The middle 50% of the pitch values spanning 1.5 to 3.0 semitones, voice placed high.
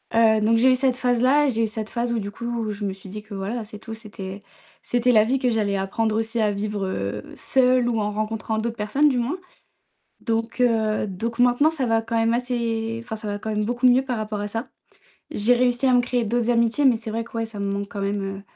Yes: narrow, 2.5 semitones; high, 225 Hz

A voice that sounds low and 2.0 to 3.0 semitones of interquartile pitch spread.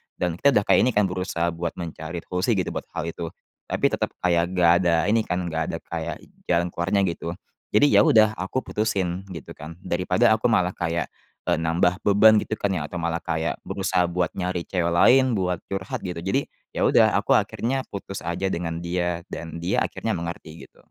Yes: very low, 90 Hz; narrow, 2.6 semitones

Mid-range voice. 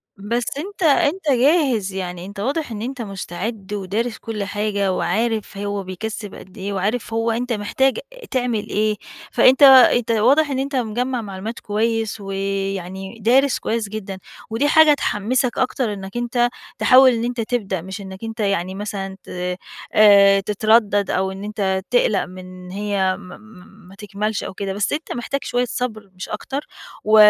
No: high, 215 Hz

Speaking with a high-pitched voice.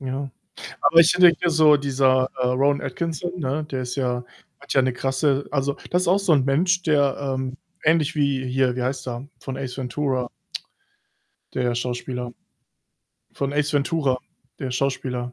No: low, 135 Hz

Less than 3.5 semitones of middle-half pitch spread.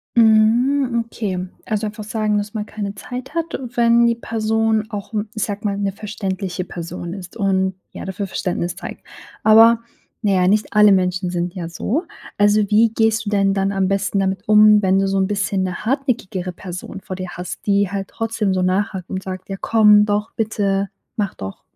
Yes: narrow, 2.5 semitones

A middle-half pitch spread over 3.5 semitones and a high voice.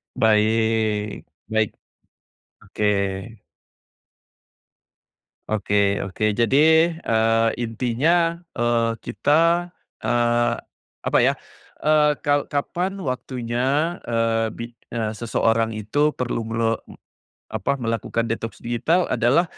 No: average, 4.0 semitones; low, 115 Hz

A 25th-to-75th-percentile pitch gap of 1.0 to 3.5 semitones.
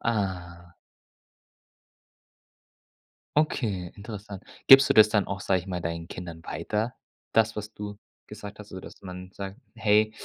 Yes: average, 2.9 semitones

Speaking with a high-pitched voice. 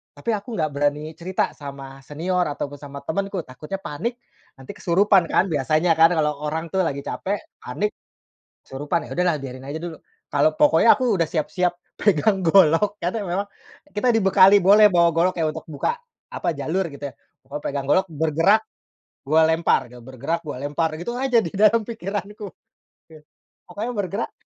No: medium, 170 Hz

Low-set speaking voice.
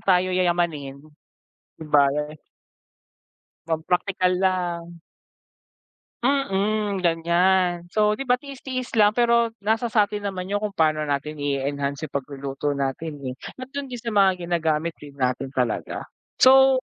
No: medium, 180 Hz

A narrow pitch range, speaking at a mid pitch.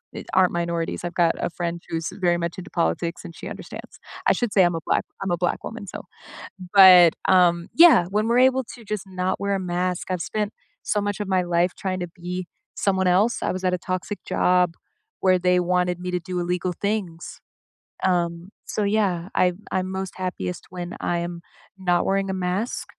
Yes: narrow, 1.8 semitones; medium, 180 Hz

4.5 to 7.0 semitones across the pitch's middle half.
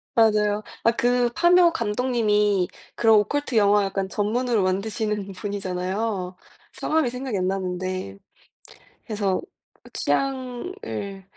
No: average, 4.0 semitones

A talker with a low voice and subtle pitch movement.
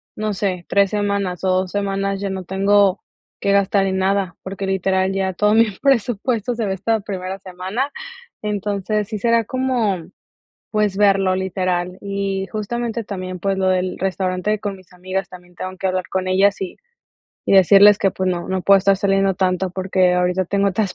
No: high, 195 Hz; narrow, 1.5 semitones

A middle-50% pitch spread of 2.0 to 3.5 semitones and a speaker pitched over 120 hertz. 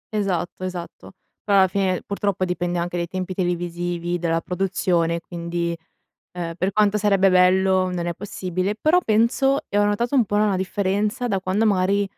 Yes: narrow, 2.5 semitones; medium, 185 Hz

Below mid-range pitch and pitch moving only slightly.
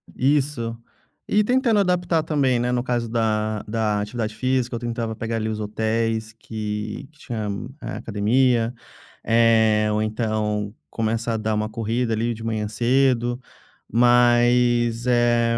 Yes: low, 115 Hz; narrow, 2.0 semitones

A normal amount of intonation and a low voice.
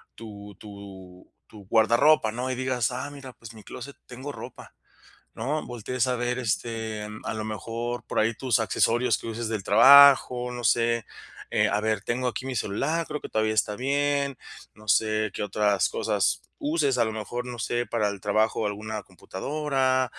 Yes: average, 3.1 semitones; low, 115 Hz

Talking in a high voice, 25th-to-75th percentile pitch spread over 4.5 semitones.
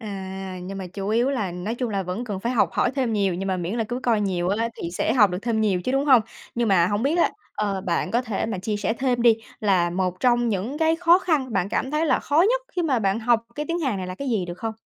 Yes: high, 220 Hz; average, 4.9 semitones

